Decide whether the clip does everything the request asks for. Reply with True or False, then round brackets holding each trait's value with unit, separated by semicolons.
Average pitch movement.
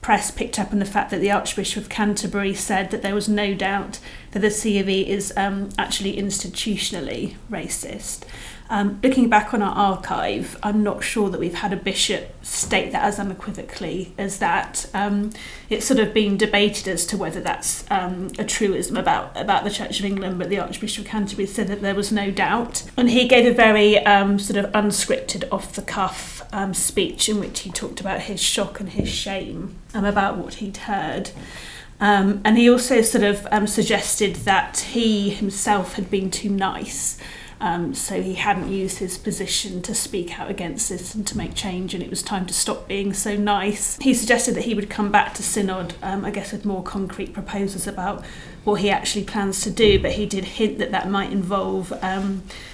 False (1.4 semitones)